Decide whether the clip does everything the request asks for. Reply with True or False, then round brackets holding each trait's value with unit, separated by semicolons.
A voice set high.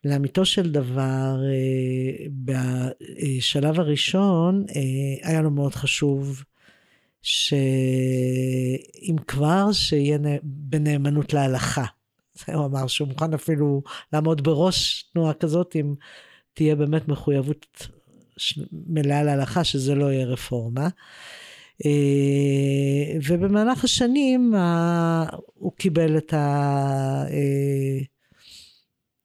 False (145 Hz)